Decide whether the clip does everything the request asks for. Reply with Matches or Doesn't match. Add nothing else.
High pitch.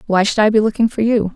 Matches